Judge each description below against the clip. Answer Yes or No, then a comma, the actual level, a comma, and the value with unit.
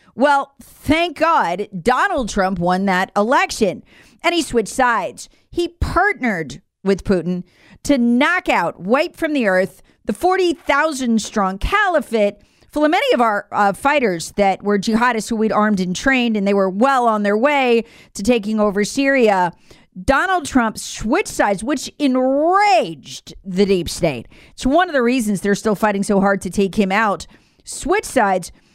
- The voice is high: Yes, high, 230 Hz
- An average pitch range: No, wide, 6.4 semitones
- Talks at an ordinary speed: Yes, average, 165 wpm